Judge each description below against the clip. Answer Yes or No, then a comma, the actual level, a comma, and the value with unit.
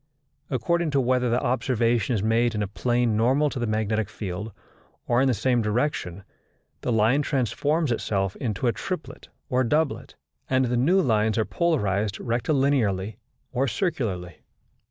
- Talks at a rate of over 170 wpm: No, average, 155 wpm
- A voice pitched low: Yes, low, 120 Hz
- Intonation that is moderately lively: Yes, average, 3.9 semitones